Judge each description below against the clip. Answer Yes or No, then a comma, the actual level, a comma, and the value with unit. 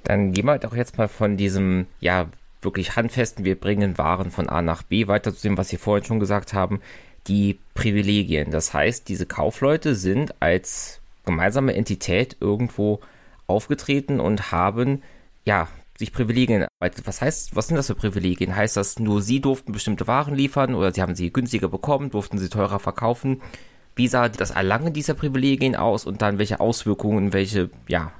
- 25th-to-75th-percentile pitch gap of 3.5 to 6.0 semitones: Yes, average, 4.2 semitones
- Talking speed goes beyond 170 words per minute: Yes, average, 180 wpm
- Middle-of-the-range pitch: No, low, 105 Hz